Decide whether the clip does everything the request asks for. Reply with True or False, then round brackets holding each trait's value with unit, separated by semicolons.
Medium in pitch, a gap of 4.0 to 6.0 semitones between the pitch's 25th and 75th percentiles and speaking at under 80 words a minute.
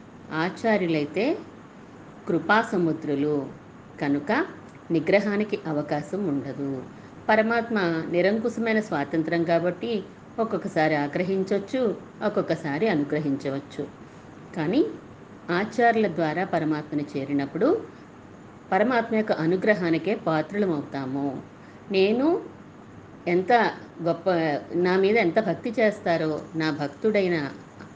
True (170 Hz; 5.6 semitones; 70 wpm)